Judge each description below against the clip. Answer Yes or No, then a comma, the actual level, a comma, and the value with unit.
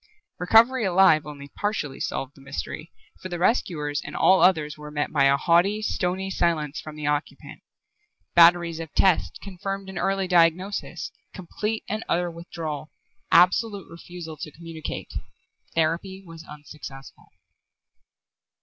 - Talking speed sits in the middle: No, slow, 130 wpm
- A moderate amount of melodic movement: Yes, average, 3.9 semitones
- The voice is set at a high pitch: No, medium, 170 Hz